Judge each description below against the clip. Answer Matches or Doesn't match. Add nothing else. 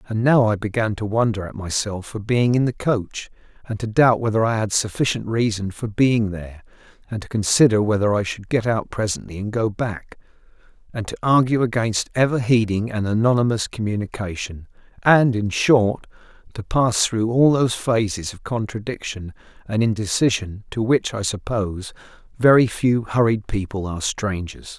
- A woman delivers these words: Doesn't match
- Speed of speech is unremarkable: Matches